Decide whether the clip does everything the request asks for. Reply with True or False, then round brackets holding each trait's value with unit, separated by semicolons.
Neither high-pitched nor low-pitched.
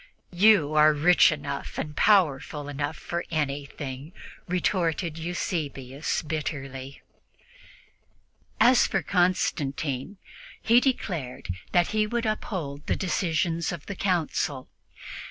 True (160 Hz)